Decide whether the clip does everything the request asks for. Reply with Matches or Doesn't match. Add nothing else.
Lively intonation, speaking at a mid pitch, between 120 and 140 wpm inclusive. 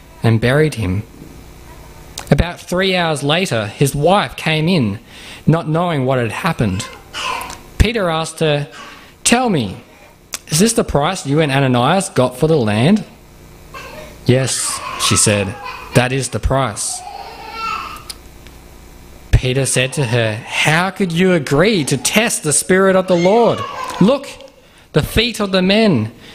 Matches